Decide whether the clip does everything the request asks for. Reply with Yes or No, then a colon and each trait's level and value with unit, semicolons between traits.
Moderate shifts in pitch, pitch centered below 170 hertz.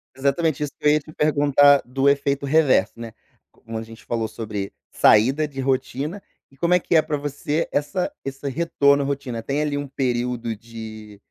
Yes: average, 3.7 semitones; medium, 140 Hz